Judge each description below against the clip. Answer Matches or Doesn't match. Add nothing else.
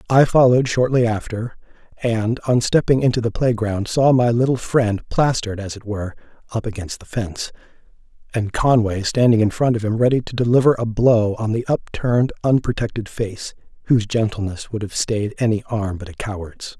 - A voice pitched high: Doesn't match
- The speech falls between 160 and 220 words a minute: Matches